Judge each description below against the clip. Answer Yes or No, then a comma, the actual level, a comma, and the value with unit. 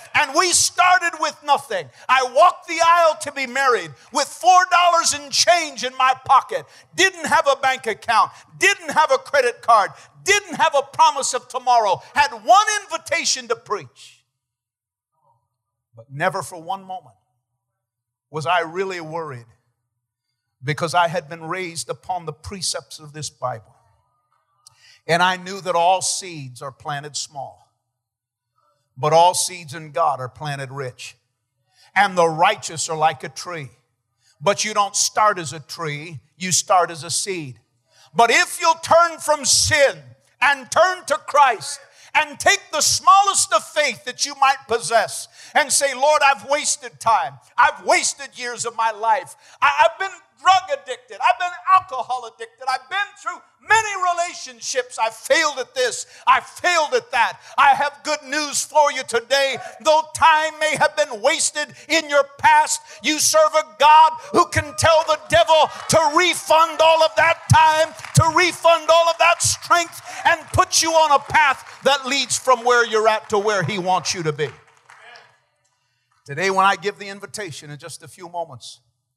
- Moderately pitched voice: No, very high, 255 Hz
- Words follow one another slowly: No, average, 165 wpm